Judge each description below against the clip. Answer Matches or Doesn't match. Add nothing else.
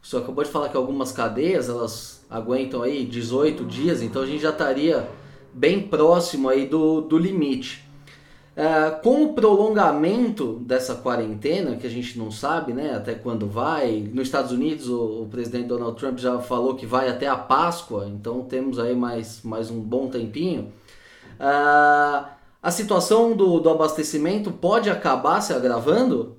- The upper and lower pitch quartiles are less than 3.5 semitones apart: Doesn't match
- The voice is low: Matches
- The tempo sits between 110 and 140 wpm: Doesn't match